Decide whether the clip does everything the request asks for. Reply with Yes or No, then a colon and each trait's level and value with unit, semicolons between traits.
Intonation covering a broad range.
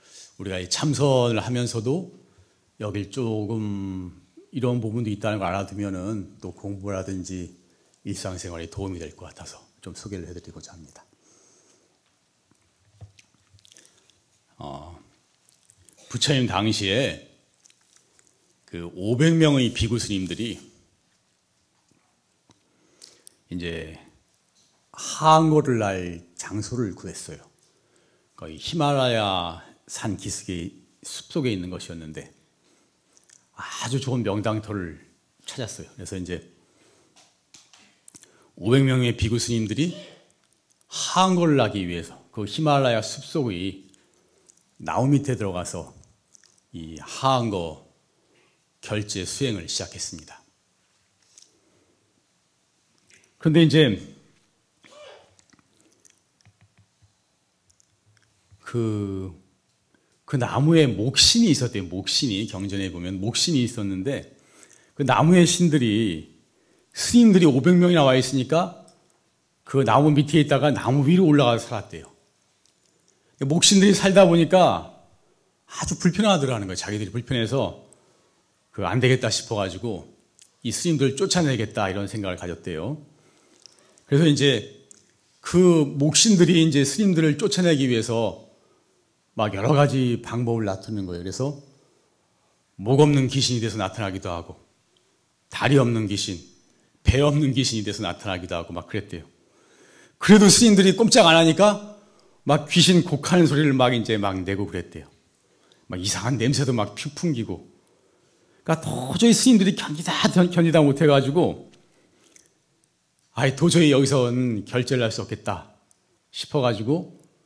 Yes: wide, 7.2 semitones